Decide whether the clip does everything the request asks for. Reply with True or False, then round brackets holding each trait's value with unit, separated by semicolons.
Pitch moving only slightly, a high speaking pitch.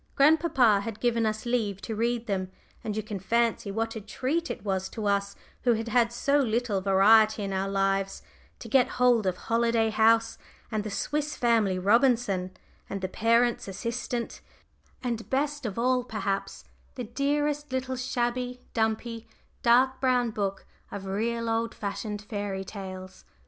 False (3.4 semitones; 225 Hz)